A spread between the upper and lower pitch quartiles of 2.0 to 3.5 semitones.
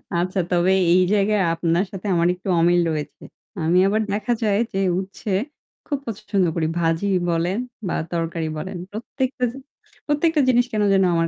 No: average, 3.9 semitones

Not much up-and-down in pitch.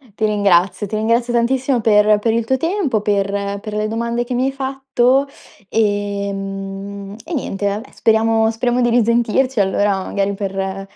No: average, 3.2 semitones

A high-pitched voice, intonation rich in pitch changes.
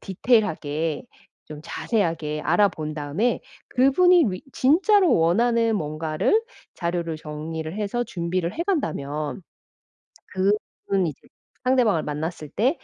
No: medium, 180 Hz; wide, 7.4 semitones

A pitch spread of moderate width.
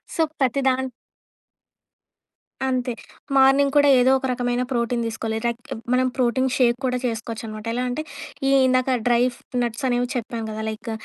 No: narrow, 1.7 semitones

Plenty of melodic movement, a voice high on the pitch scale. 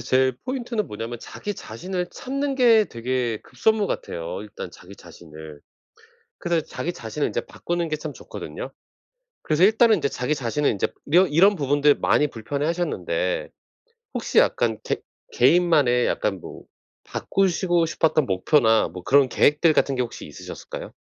No: wide, 7.7 semitones; medium, 150 Hz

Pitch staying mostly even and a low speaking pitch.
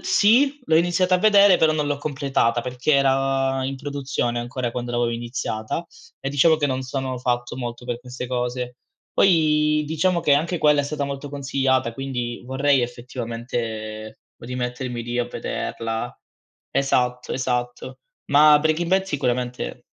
No: average, 3.5 semitones; low, 130 Hz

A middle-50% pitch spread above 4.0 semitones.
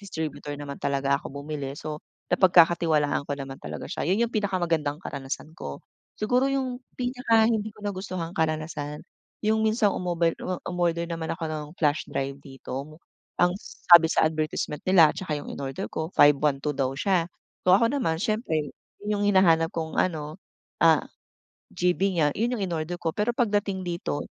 Yes: average, 4.9 semitones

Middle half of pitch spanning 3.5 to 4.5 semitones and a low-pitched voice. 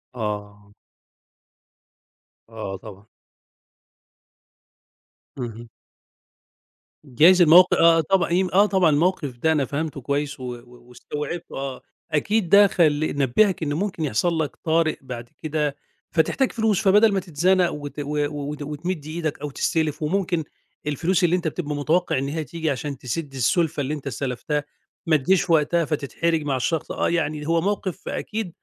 No: average, 3.8 semitones; medium, 155 Hz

